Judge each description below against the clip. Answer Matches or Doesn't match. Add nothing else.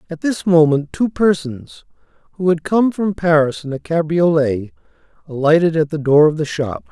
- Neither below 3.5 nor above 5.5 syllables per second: Matches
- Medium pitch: Matches